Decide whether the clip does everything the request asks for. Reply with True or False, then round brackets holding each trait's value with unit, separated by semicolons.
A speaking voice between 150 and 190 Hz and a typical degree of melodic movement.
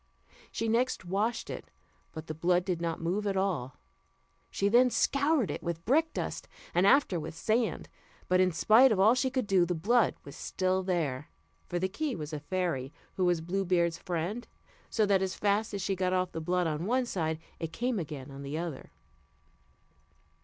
True (185 Hz; 4.6 semitones)